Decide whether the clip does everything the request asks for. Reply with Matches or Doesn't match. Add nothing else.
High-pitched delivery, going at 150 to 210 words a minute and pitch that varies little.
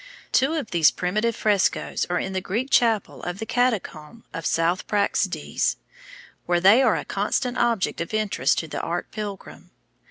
Doesn't match